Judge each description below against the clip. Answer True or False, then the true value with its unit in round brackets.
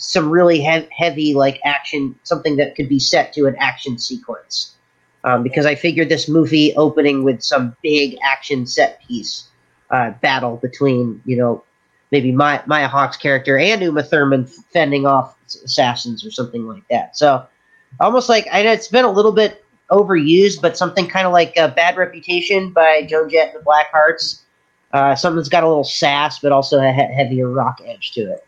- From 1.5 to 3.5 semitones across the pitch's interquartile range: False (3.9 semitones)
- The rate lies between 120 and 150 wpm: False (190 wpm)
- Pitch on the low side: False (150 Hz)